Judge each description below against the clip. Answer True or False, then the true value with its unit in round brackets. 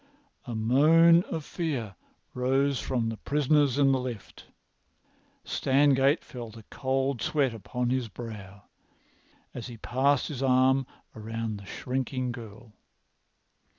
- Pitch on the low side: True (130 Hz)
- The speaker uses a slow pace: True (120 wpm)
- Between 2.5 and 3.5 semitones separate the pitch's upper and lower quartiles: True (3.2 semitones)